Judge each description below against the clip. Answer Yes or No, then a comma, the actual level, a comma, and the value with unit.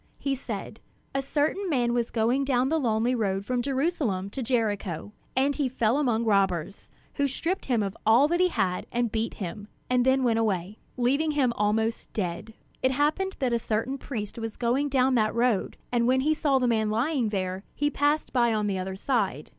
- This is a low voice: No, high, 240 Hz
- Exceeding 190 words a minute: Yes, average, 200 wpm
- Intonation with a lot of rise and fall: No, average, 4.3 semitones